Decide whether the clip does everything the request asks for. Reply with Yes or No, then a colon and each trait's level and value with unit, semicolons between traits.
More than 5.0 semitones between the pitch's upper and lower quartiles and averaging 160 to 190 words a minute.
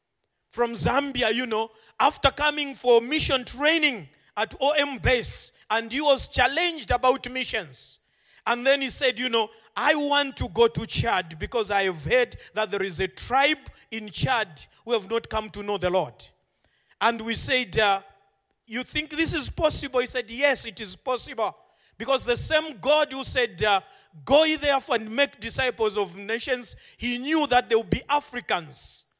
No: average, 4.3 semitones; average, 175 wpm